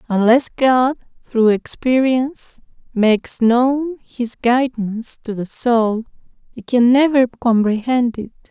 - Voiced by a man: No, female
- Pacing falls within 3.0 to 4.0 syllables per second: Yes, 3.7 syllables/s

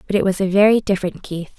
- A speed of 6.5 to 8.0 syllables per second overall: Yes, 6.9 syllables/s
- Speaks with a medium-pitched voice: No, high, 195 Hz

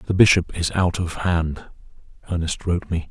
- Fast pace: No, average, 175 wpm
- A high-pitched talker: No, very low, 85 Hz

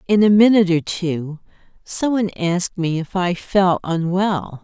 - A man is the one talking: No, female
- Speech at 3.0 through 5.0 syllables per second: Yes, 4.5 syllables/s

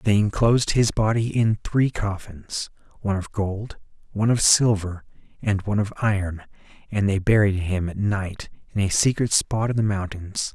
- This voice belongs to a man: Yes, male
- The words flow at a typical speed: Yes, average, 160 wpm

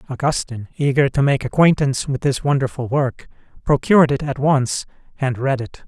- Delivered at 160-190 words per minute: Yes, average, 165 wpm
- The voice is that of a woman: No, male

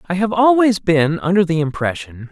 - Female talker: No, male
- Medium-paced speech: Yes, average, 180 wpm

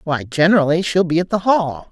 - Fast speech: Yes, fast, 220 wpm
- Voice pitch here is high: No, medium, 170 Hz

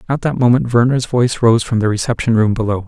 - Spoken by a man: Yes, male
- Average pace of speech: No, fast, 230 wpm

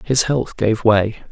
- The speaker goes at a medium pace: Yes, average, 180 wpm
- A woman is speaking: No, male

